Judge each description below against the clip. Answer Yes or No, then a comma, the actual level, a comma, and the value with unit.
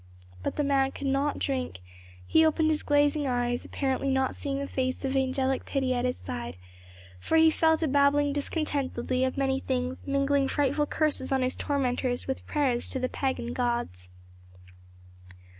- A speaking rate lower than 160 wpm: No, average, 165 wpm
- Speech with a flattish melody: Yes, narrow, 2.1 semitones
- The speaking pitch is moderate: No, very high, 270 Hz